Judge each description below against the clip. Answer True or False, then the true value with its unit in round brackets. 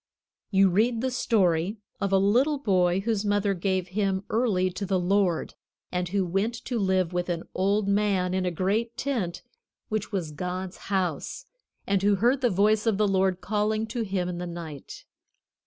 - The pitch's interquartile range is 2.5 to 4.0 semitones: True (2.8 semitones)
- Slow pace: False (180 wpm)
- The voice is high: True (195 Hz)